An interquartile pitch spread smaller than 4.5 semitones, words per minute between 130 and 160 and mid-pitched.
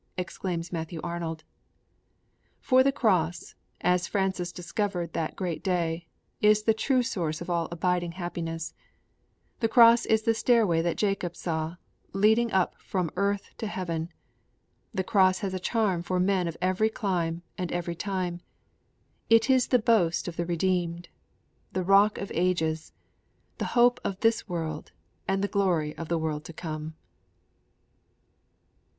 Yes: average, 3.4 semitones; average, 150 wpm; medium, 180 Hz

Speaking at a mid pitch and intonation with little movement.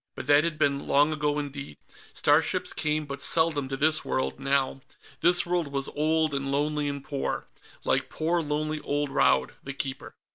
Yes: medium, 145 Hz; narrow, 1.8 semitones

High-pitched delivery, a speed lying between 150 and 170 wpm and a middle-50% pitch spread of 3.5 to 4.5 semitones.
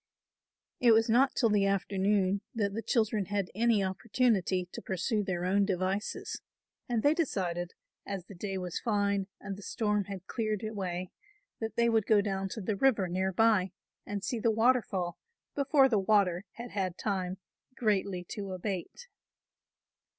No: high, 200 Hz; average, 160 wpm; average, 2.9 semitones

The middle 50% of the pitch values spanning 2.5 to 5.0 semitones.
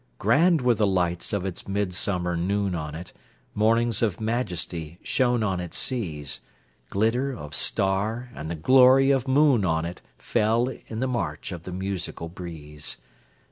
No: wide, 5.6 semitones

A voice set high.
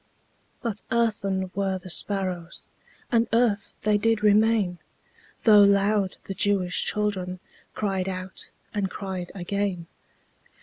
Yes: high, 200 Hz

